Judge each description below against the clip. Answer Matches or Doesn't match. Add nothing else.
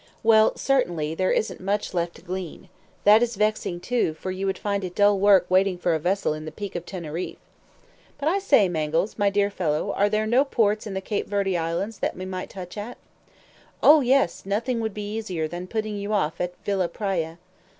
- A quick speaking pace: Matches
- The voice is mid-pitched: Doesn't match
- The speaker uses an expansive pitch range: Doesn't match